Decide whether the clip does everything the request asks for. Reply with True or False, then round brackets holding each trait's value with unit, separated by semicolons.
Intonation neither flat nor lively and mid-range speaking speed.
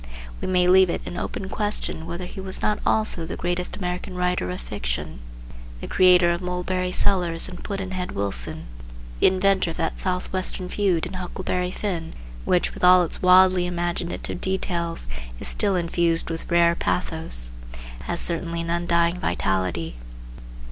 False (1.6 semitones; 155 wpm)